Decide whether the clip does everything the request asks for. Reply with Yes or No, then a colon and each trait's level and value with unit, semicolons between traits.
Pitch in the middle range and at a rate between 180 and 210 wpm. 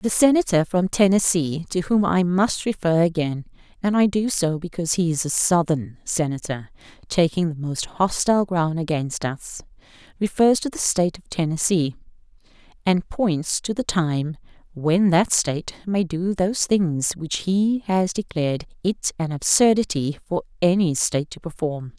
No: medium, 175 Hz; average, 150 wpm